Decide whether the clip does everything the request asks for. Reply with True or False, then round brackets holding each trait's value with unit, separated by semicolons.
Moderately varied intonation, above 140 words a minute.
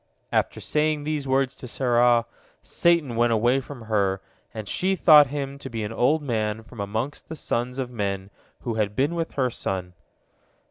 True (4.5 semitones; 180 wpm)